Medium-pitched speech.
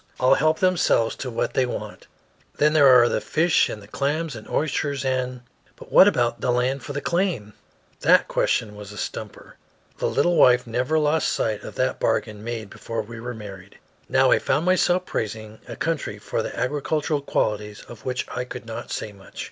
No: low, 125 Hz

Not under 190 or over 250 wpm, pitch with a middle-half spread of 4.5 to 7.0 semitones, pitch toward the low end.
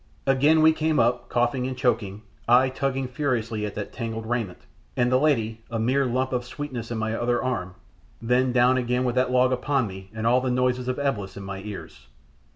No: fast, 205 wpm; narrow, 2.4 semitones; low, 125 Hz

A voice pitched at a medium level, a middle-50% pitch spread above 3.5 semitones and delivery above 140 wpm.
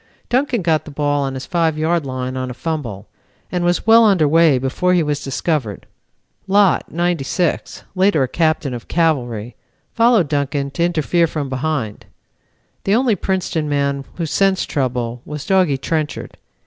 Yes: medium, 155 Hz; average, 4.4 semitones; average, 160 wpm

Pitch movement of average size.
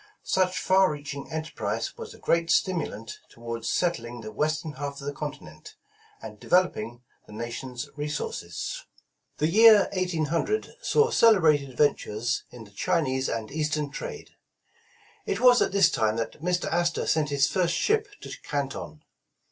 No: wide, 6.2 semitones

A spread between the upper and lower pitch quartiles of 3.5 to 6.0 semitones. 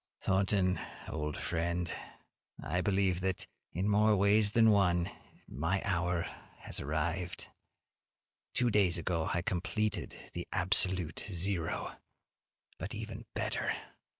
No: average, 2.9 semitones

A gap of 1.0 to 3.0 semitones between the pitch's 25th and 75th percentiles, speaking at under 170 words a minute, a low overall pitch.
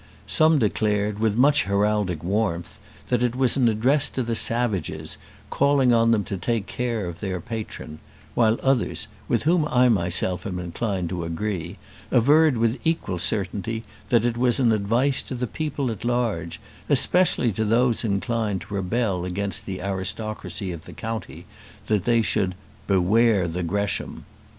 No: average, 4.3 semitones; average, 160 wpm; low, 110 Hz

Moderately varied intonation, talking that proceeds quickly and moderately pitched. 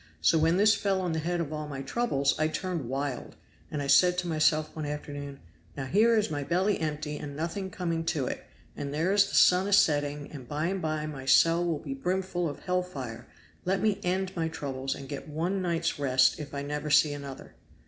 Yes: average, 4.1 semitones; fast, 220 wpm; medium, 155 Hz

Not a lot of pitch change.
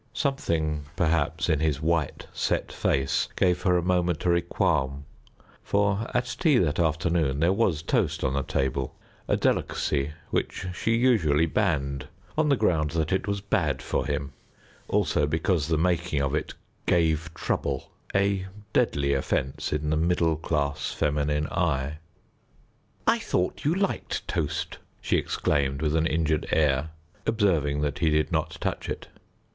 No: average, 3.7 semitones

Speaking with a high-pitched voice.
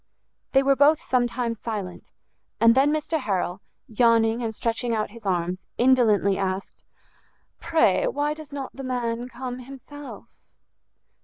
Yes: high, 240 Hz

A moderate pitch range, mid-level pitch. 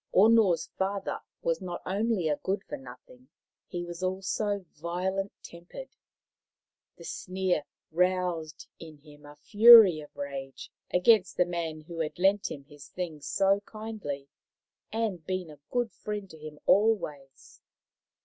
Yes: average, 4.4 semitones; medium, 180 Hz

